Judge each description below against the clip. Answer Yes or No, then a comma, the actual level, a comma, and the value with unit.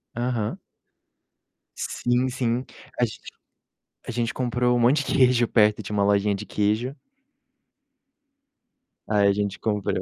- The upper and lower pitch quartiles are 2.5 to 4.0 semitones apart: Yes, average, 2.9 semitones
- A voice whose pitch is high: No, low, 115 Hz